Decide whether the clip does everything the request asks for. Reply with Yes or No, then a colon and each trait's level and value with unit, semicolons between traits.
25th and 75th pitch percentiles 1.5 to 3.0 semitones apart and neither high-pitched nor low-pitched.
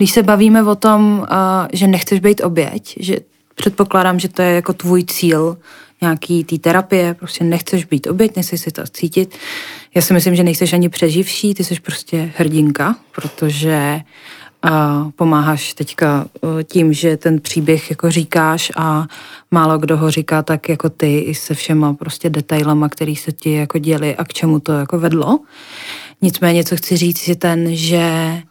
Yes: narrow, 2.4 semitones; medium, 170 Hz